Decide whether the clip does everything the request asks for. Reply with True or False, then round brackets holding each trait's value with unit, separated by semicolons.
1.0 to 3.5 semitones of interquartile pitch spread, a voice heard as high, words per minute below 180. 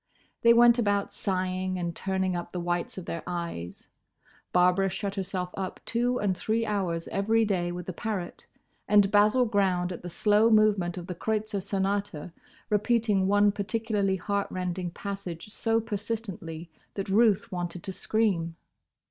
True (2.9 semitones; 195 Hz; 155 wpm)